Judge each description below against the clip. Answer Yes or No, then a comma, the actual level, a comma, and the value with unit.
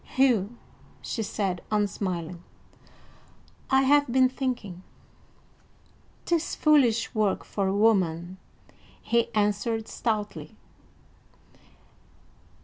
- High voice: Yes, high, 215 Hz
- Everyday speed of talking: No, slow, 80 wpm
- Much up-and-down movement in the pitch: No, average, 4.6 semitones